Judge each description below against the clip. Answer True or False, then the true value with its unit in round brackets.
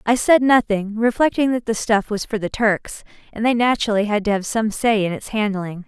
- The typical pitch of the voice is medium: False (220 Hz)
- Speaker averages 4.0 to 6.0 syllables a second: True (5.3 syllables/s)